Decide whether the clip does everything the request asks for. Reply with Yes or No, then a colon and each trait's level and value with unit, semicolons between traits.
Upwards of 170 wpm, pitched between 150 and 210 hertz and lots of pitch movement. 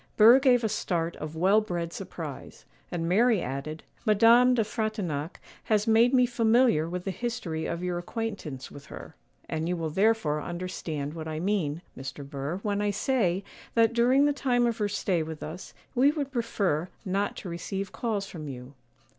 Yes: average, 180 wpm; high, 190 Hz; wide, 6.1 semitones